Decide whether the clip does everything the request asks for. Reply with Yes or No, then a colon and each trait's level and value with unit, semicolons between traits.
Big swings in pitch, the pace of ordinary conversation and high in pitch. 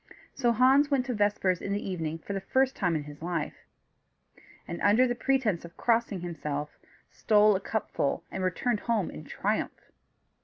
Yes: wide, 5.8 semitones; average, 165 wpm; high, 200 Hz